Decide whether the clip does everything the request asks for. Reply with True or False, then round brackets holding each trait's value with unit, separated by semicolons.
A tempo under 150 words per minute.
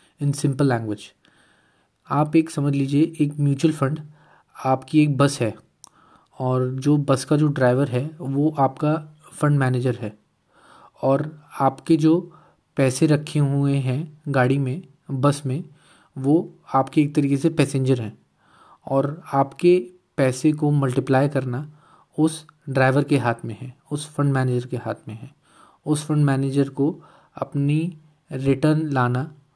True (140 wpm)